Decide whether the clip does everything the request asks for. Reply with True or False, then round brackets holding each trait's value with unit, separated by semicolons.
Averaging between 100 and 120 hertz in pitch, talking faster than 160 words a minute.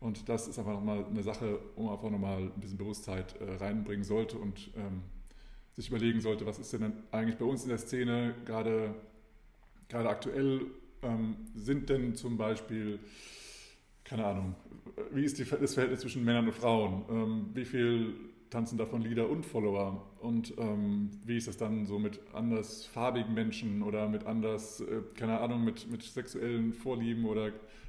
True (110 Hz; 170 wpm)